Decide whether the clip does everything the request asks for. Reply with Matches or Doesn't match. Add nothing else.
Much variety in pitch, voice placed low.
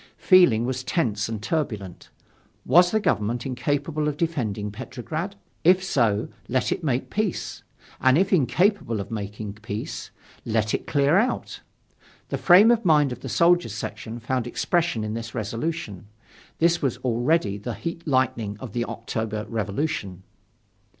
Matches